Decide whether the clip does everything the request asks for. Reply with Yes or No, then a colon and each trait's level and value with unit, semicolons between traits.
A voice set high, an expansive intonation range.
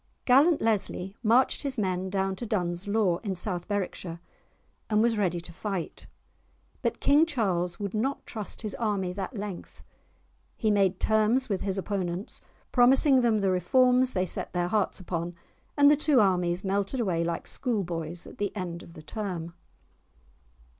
No: high, 200 Hz; average, 4.1 semitones